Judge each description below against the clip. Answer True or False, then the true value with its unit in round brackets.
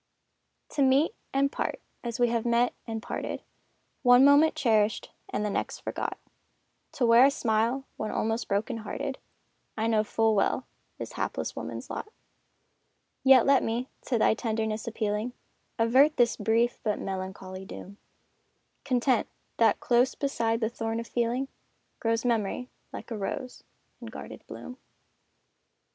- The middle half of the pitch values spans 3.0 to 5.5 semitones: False (2.6 semitones)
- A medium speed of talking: True (145 wpm)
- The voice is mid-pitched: False (230 Hz)